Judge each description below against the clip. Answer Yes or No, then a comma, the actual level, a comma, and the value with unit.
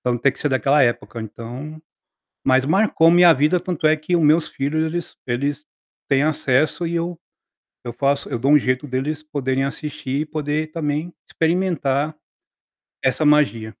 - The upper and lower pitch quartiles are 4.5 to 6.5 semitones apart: No, average, 3.0 semitones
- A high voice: No, medium, 150 Hz